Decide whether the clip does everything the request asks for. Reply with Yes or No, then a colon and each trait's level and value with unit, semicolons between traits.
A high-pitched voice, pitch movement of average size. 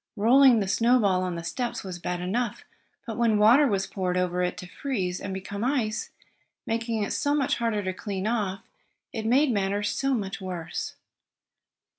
Yes: high, 210 Hz; average, 4.1 semitones